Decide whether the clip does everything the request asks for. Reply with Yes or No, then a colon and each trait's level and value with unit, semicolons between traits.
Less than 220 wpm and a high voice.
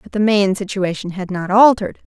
Yes: average, 200 wpm; high, 200 Hz